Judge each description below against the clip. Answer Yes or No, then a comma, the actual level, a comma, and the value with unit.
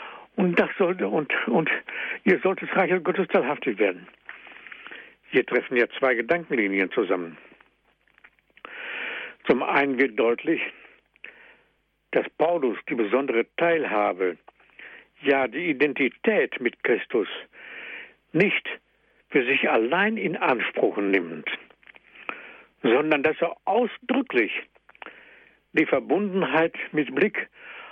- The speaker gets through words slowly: Yes, slow, 100 wpm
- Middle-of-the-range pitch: Yes, medium, 170 Hz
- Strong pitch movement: Yes, wide, 8.5 semitones